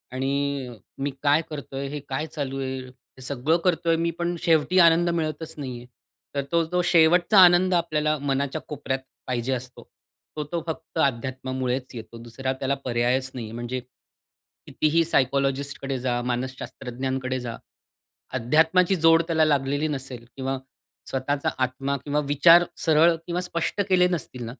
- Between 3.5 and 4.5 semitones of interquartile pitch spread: Yes, average, 3.9 semitones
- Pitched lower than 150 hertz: Yes, medium, 140 Hz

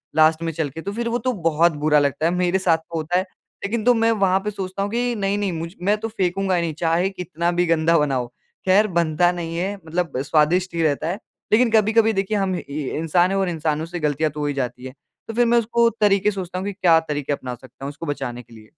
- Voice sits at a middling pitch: Yes, medium, 175 Hz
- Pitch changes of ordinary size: Yes, average, 4.1 semitones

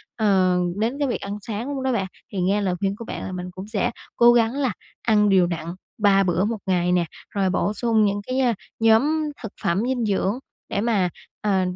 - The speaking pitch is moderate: No, high, 205 Hz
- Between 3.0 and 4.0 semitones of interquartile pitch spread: Yes, average, 3.6 semitones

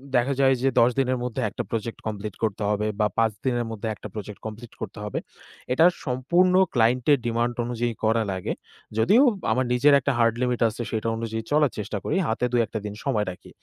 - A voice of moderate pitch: No, low, 115 Hz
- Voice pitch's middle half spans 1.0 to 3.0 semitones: Yes, average, 2.7 semitones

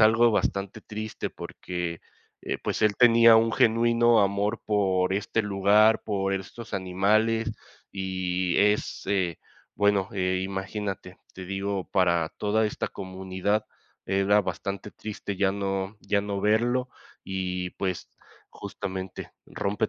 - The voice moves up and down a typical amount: No, narrow, 2.2 semitones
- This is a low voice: Yes, low, 100 Hz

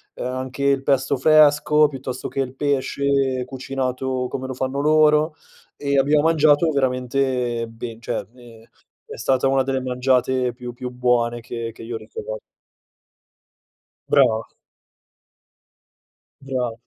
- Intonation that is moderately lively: No, narrow, 2.1 semitones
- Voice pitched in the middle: No, low, 130 Hz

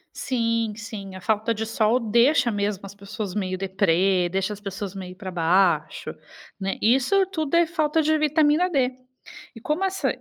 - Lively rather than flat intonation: Yes, wide, 6.7 semitones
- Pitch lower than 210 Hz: No, high, 215 Hz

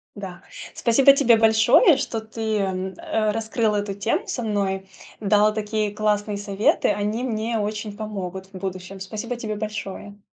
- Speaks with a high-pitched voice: Yes, high, 215 Hz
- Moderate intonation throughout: No, narrow, 1.8 semitones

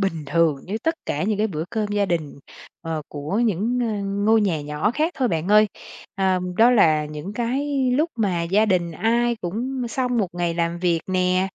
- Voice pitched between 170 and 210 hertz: Yes, high, 195 Hz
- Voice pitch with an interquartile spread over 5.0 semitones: Yes, wide, 5.4 semitones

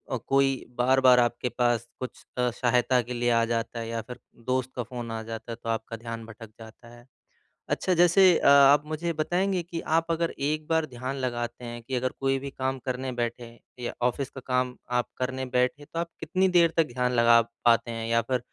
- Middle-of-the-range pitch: No, low, 125 Hz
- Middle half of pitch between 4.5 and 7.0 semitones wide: No, average, 2.9 semitones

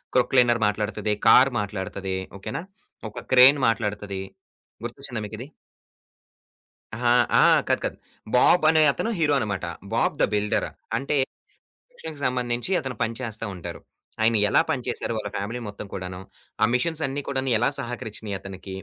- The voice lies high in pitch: No, low, 115 Hz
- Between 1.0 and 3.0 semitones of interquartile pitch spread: No, average, 4.2 semitones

